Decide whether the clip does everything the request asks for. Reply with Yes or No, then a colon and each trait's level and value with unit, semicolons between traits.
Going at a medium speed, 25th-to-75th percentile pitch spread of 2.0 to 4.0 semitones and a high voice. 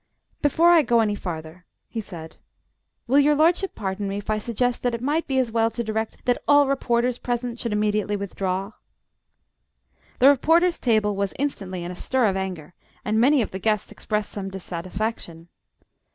No: average, 180 wpm; average, 4.6 semitones; high, 220 Hz